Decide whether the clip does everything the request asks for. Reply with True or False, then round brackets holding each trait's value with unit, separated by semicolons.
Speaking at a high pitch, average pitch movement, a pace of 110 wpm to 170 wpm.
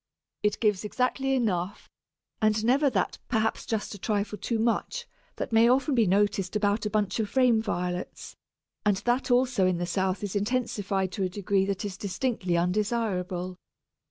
True (210 Hz; 3.5 semitones; 165 wpm)